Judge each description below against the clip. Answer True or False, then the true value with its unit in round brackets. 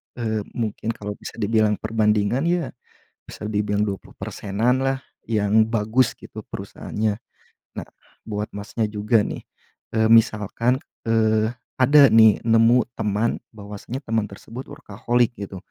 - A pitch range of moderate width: False (2.0 semitones)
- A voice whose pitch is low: True (110 Hz)